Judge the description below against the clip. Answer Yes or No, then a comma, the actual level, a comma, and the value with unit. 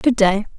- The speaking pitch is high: Yes, high, 210 Hz